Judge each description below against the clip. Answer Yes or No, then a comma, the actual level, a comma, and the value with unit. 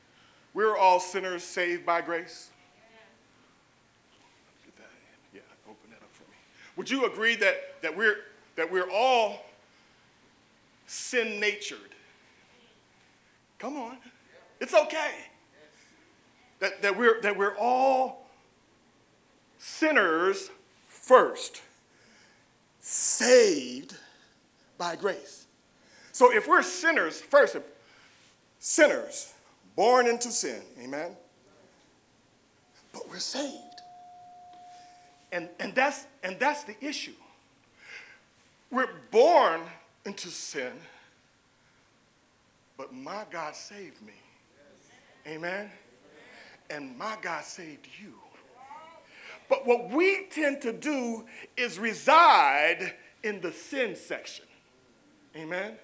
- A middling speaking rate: No, slow, 95 wpm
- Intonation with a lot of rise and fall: Yes, wide, 8.3 semitones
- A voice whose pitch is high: Yes, very high, 255 Hz